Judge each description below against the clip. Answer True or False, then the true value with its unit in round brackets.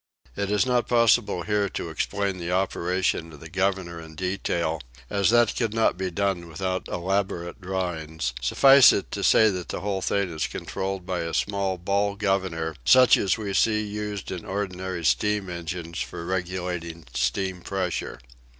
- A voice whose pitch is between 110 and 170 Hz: False (95 Hz)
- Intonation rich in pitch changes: False (2.8 semitones)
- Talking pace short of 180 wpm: True (165 wpm)